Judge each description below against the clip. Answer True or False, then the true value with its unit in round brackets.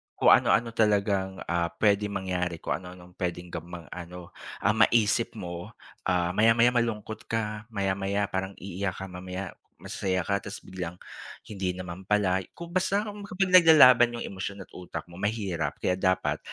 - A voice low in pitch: True (95 Hz)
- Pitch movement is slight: False (3.3 semitones)